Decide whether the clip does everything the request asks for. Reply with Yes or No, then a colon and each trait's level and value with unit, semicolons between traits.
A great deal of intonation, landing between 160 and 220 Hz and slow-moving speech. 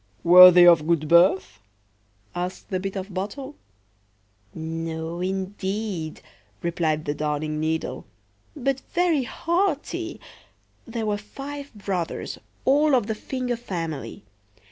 Yes: wide, 7.0 semitones; medium, 185 Hz; slow, 110 wpm